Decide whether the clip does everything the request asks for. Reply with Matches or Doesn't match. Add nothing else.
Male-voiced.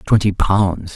Matches